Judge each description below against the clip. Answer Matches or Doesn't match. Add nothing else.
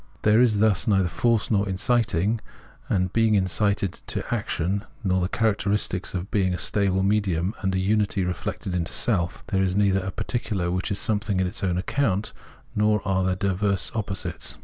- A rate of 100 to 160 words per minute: Doesn't match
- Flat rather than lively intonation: Matches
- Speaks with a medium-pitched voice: Doesn't match